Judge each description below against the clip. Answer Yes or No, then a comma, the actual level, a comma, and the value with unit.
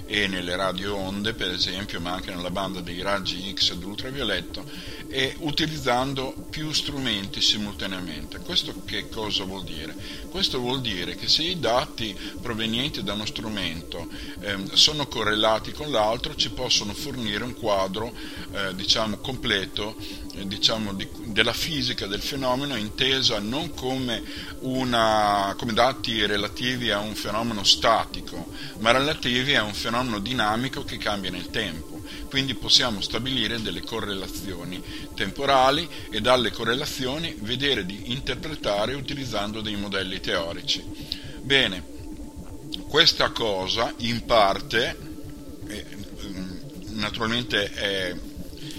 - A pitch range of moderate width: Yes, average, 4.7 semitones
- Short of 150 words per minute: Yes, average, 120 wpm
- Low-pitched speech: Yes, low, 110 Hz